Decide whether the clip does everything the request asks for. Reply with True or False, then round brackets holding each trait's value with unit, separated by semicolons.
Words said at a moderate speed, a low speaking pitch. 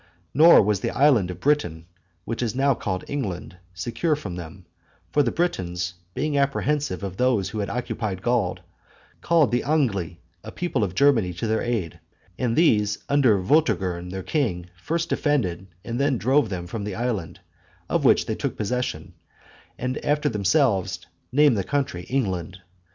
True (160 wpm; 110 Hz)